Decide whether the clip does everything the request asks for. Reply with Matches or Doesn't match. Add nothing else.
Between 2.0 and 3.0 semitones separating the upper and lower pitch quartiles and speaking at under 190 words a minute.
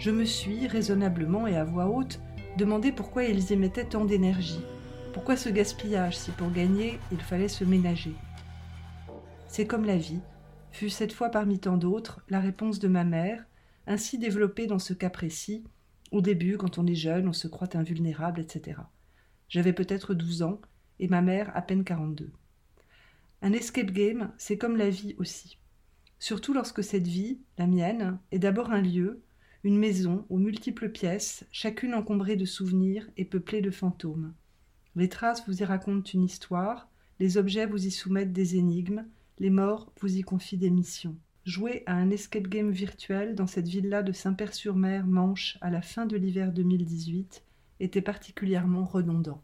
Matches